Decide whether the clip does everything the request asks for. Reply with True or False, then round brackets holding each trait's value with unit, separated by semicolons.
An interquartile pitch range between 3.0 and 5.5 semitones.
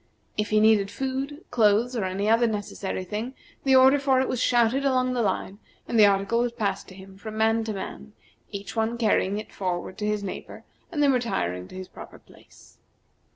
True (3.8 semitones)